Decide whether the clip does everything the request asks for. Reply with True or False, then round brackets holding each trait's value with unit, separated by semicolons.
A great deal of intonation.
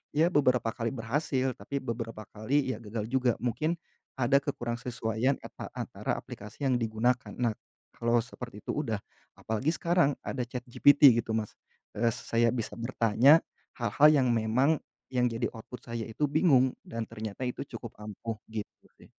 False (2.9 semitones)